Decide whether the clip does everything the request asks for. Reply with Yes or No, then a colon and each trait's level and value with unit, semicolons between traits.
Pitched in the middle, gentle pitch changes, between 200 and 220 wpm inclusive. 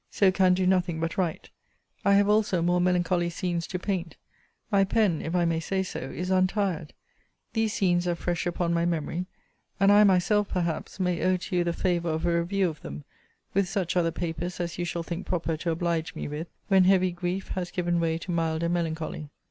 Yes: medium, 175 Hz; narrow, 1.9 semitones; fast, 205 wpm